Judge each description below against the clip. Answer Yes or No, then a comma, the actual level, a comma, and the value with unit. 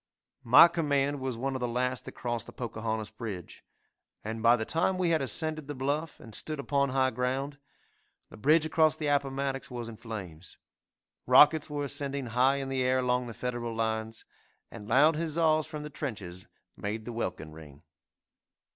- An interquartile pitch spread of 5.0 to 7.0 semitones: No, average, 4.3 semitones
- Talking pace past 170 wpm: Yes, average, 180 wpm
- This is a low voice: Yes, low, 130 Hz